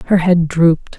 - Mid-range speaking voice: Yes, medium, 170 Hz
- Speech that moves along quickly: No, average, 185 wpm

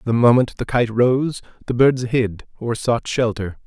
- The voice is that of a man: Yes, male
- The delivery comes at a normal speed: Yes, average, 180 wpm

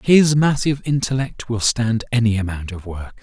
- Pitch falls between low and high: No, low, 120 Hz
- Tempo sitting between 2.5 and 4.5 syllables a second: No, 5.0 syllables/s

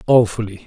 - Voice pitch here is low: Yes, low, 105 Hz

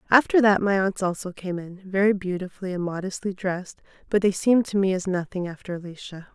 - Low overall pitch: No, high, 190 Hz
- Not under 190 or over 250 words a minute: Yes, average, 200 wpm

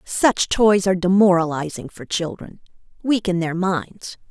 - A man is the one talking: No, female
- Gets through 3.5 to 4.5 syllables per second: Yes, 4.3 syllables/s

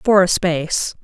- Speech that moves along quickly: No, average, 175 wpm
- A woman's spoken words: Yes, female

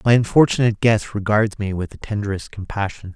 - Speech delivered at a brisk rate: No, average, 170 wpm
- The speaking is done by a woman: No, male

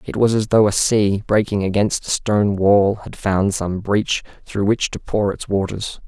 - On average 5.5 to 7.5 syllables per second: No, 4.4 syllables/s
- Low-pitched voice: Yes, low, 100 Hz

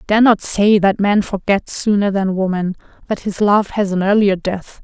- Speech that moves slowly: No, average, 200 wpm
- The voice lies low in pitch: No, high, 200 Hz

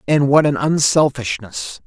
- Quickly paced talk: No, slow, 130 wpm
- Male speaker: Yes, male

